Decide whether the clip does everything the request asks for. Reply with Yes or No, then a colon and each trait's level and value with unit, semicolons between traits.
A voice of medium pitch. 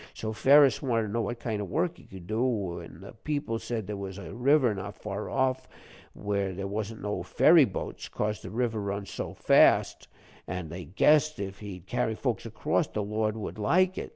No: low, 105 Hz